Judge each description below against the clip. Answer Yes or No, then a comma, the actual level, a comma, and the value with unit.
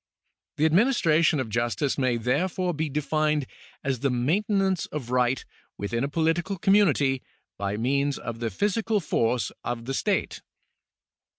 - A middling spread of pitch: No, wide, 5.8 semitones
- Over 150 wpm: No, slow, 135 wpm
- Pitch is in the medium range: Yes, medium, 145 Hz